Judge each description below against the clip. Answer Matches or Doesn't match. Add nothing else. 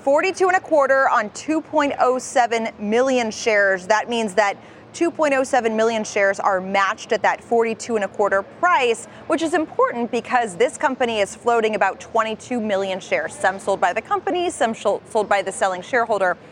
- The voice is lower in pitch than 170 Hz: Doesn't match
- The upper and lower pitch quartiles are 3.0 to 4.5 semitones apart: Doesn't match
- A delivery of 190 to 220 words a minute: Doesn't match